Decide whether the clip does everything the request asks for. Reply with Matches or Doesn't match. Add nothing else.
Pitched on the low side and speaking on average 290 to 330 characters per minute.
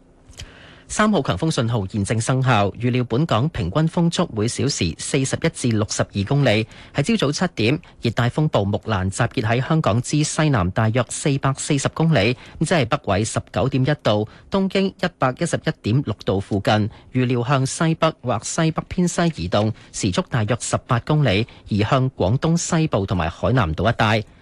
Doesn't match